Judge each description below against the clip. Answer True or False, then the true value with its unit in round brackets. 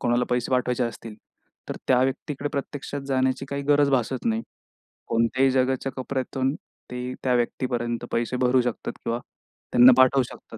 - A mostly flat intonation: True (1.7 semitones)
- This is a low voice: True (130 Hz)